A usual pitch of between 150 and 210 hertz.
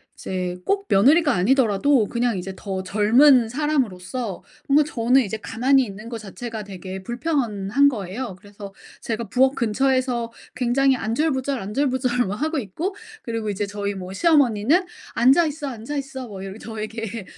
No: high, 235 Hz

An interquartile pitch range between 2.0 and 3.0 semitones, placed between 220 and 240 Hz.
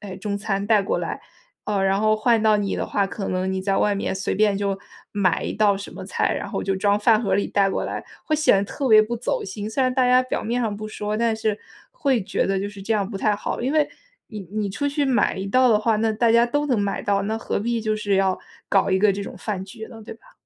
No: narrow, 2.5 semitones; high, 210 Hz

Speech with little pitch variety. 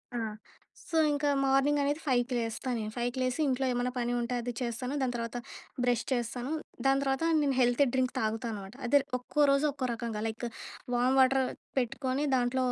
Yes: narrow, 2.1 semitones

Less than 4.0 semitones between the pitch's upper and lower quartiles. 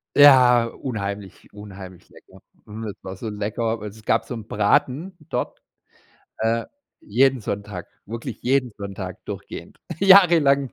No: average, 4.3 semitones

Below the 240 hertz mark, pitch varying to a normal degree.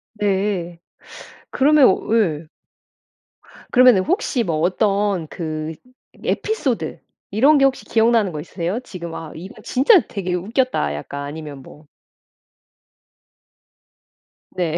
No: high, 190 Hz; wide, 6.6 semitones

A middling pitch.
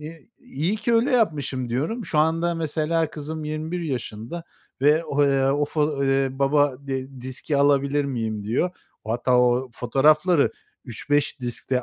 Yes: medium, 145 Hz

